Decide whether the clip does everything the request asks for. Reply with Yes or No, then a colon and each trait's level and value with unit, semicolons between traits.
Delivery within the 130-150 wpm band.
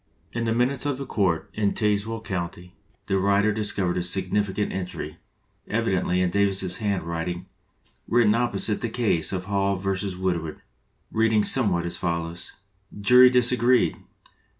Yes: average, 140 wpm